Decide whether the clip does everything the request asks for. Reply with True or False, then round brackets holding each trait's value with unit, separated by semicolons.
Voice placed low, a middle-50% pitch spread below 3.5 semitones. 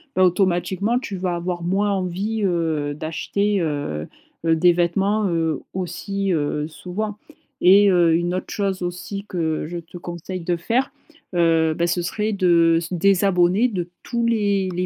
False (180 Hz; 2.8 semitones)